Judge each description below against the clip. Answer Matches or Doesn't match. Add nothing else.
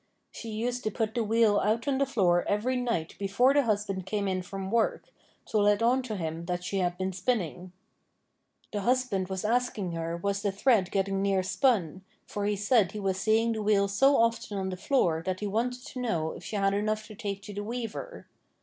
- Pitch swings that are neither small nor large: Matches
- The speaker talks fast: Matches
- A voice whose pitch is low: Doesn't match